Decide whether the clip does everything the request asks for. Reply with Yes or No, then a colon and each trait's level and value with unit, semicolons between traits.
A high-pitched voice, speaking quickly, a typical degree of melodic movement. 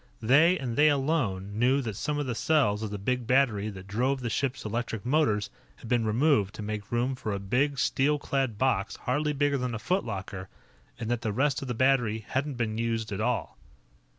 No: low, 120 Hz; fast, 210 wpm; average, 4.3 semitones